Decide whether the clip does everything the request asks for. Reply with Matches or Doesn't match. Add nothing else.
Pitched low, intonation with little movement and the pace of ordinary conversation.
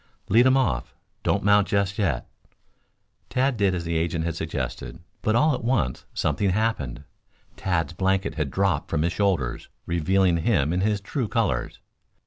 Doesn't match